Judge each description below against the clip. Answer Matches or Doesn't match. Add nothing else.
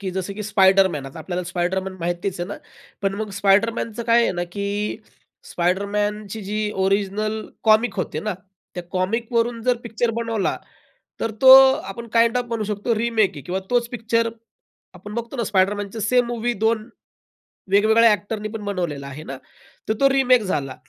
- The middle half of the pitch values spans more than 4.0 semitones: Doesn't match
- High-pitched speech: Matches